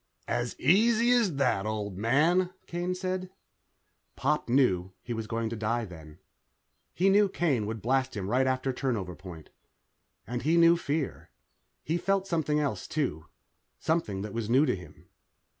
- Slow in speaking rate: No, average, 160 wpm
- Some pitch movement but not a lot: No, wide, 7.8 semitones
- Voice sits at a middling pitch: No, low, 130 Hz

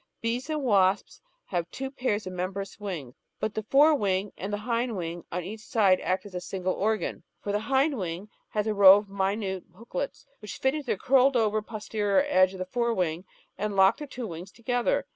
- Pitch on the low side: No, high, 205 Hz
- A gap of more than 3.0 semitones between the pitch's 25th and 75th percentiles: Yes, average, 4.0 semitones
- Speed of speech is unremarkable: No, fast, 215 wpm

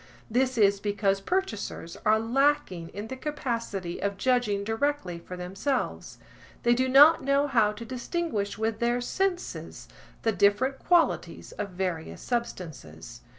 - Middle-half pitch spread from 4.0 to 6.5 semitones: Yes, average, 5.0 semitones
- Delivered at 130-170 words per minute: Yes, slow, 135 wpm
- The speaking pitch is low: No, high, 225 Hz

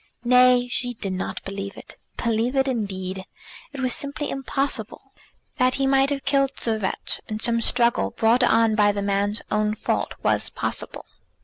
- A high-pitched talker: Yes, high, 235 Hz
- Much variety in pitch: No, average, 3.8 semitones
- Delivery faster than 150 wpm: Yes, average, 170 wpm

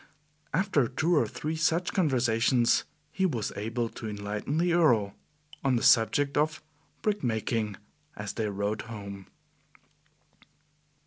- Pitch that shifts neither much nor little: No, wide, 6.6 semitones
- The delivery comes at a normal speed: No, slow, 125 wpm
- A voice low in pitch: Yes, low, 120 Hz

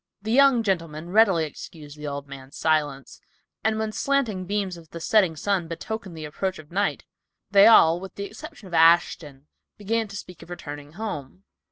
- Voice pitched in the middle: Yes, medium, 175 Hz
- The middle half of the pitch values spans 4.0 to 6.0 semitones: Yes, average, 5.2 semitones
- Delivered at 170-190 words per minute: Yes, average, 185 wpm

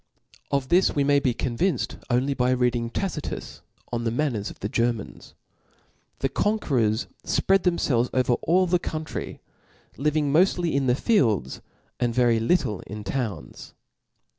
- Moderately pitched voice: No, low, 130 Hz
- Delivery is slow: No, average, 150 wpm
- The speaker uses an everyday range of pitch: Yes, average, 5.0 semitones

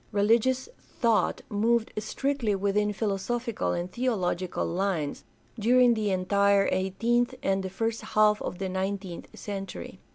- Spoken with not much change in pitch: No, average, 3.3 semitones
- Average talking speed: No, slow, 125 wpm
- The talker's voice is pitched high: Yes, high, 205 Hz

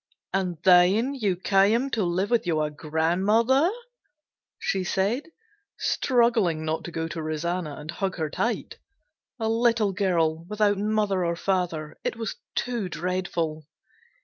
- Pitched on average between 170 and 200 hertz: Yes, medium, 185 Hz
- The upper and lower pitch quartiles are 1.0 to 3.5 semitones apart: No, average, 4.7 semitones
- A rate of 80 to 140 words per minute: Yes, slow, 135 wpm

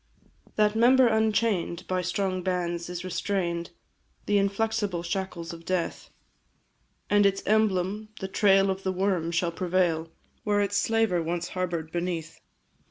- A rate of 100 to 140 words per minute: Yes, slow, 135 wpm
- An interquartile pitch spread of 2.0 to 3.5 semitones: Yes, average, 2.9 semitones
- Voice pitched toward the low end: No, medium, 185 Hz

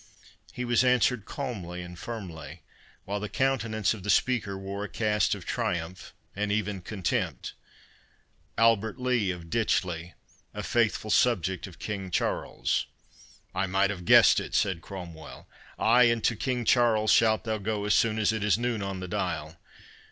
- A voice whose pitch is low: Yes, low, 105 Hz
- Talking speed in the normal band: Yes, average, 160 wpm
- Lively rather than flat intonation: No, average, 3.8 semitones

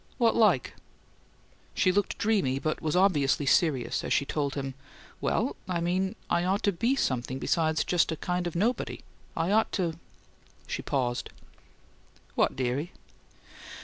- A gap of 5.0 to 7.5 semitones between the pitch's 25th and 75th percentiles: Yes, average, 5.3 semitones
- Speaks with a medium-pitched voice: Yes, medium, 170 Hz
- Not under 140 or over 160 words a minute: Yes, average, 150 wpm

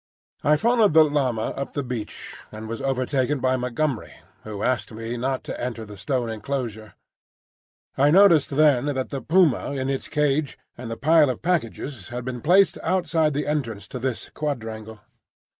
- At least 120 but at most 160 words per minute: No, average, 170 wpm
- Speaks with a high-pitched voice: No, low, 130 Hz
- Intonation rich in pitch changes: No, average, 4.3 semitones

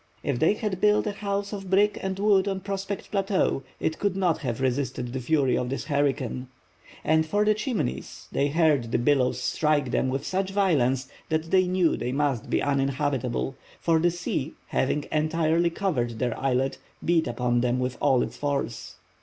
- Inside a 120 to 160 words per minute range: No, average, 180 wpm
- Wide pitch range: Yes, wide, 6.5 semitones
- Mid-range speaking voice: Yes, medium, 150 Hz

